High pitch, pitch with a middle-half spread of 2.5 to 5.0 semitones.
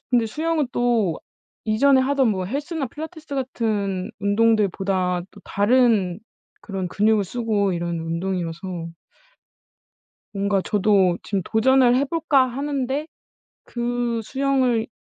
No: high, 225 Hz; wide, 5.4 semitones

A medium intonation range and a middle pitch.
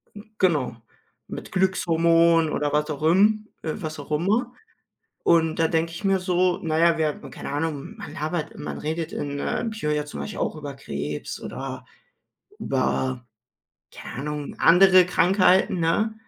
Yes: average, 3.8 semitones; medium, 165 Hz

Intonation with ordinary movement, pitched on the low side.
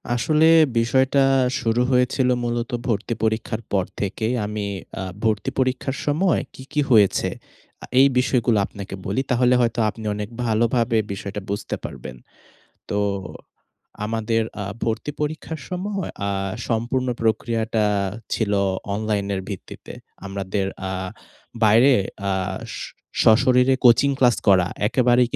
Yes: average, 3.3 semitones; low, 115 Hz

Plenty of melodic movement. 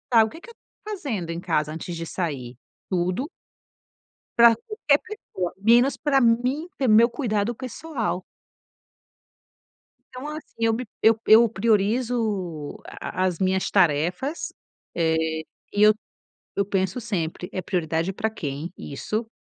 Yes: wide, 5.8 semitones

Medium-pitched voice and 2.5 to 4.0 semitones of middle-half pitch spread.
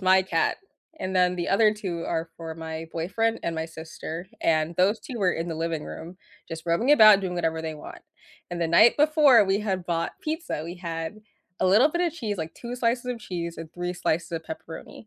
No: medium, 175 Hz; average, 4.6 semitones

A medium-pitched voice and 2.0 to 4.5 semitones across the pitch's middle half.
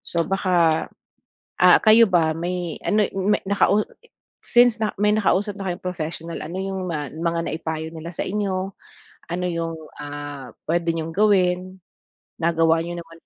Yes: medium, 175 Hz; average, 2.9 semitones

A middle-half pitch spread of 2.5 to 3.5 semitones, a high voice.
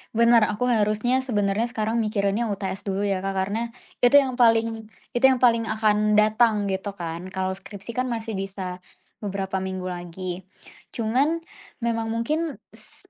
Yes: average, 3.2 semitones; high, 215 Hz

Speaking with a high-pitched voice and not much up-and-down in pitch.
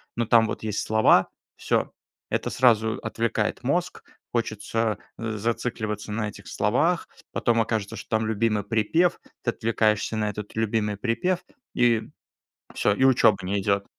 No: low, 110 Hz; narrow, 1.7 semitones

